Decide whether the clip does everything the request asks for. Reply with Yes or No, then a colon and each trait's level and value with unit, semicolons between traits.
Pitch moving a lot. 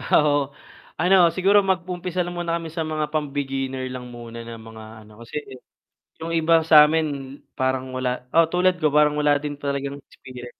No: average, 4.1 semitones